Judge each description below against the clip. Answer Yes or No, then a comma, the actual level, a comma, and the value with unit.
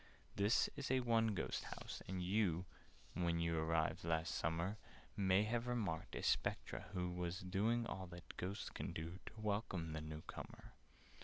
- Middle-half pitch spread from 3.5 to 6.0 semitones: Yes, average, 4.3 semitones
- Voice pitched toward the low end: Yes, very low, 95 Hz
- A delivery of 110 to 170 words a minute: Yes, average, 165 wpm